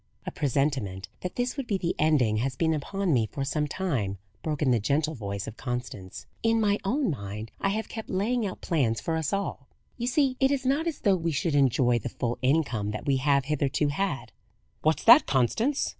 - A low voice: No, medium, 150 Hz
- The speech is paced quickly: Yes, fast, 210 wpm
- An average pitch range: No, wide, 8.2 semitones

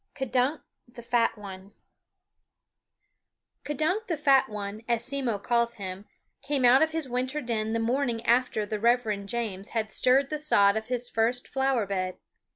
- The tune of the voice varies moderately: Yes, average, 3.7 semitones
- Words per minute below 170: Yes, average, 160 wpm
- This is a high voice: Yes, high, 240 Hz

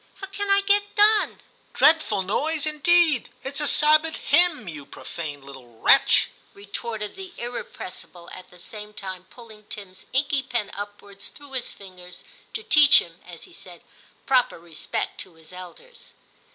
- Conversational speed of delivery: Yes, average, 165 wpm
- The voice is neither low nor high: No, high, 235 Hz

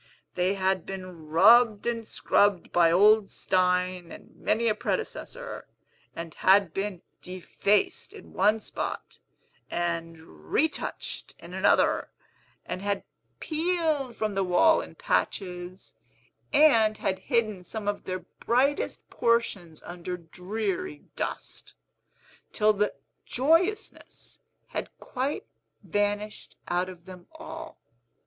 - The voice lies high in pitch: Yes, high, 200 Hz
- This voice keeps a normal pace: No, slow, 115 wpm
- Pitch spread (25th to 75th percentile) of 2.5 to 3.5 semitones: No, average, 4.1 semitones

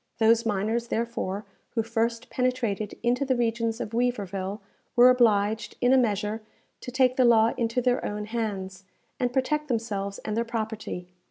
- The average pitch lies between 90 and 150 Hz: No, high, 230 Hz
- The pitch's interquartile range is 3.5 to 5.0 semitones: No, average, 2.7 semitones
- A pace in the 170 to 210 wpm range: No, average, 160 wpm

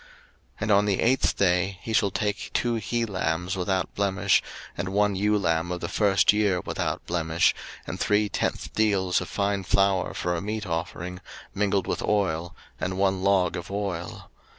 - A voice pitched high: No, very low, 95 Hz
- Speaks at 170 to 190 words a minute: Yes, average, 175 wpm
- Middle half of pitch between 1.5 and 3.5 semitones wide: Yes, narrow, 2.4 semitones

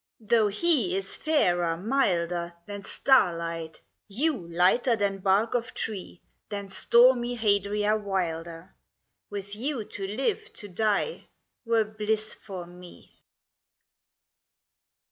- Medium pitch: No, high, 205 Hz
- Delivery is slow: Yes, slow, 110 wpm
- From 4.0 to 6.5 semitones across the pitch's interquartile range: Yes, average, 4.3 semitones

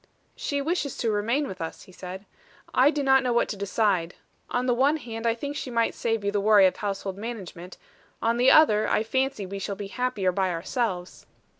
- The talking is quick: Yes, fast, 210 wpm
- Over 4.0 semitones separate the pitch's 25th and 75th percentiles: Yes, average, 4.5 semitones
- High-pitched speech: Yes, high, 225 Hz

